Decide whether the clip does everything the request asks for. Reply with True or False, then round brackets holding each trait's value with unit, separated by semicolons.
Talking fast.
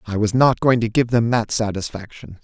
True (220 wpm)